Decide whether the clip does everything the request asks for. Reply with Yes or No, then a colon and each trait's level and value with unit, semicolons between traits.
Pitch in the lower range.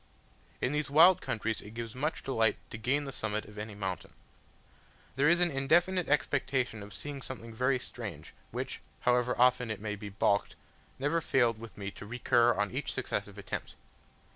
Yes: low, 125 Hz